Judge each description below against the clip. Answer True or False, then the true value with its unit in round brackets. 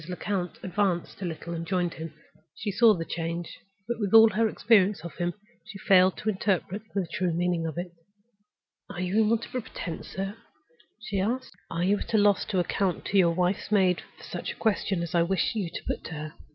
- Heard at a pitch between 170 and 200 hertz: True (185 Hz)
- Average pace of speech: False (220 wpm)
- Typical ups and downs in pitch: True (3.1 semitones)